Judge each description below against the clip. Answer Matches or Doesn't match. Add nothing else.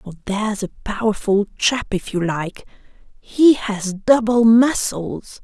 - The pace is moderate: Doesn't match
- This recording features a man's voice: Doesn't match